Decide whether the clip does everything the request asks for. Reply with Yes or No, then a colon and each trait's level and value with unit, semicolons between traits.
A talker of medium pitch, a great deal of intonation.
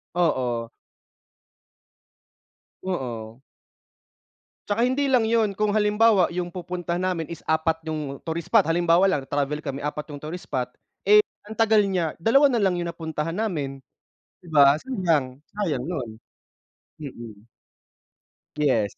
Yes: medium, 165 Hz; wide, 5.8 semitones